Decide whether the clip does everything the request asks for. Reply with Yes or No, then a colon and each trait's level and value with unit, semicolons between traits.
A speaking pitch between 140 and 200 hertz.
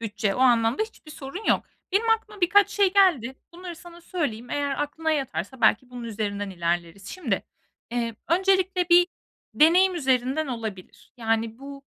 No: very high, 275 Hz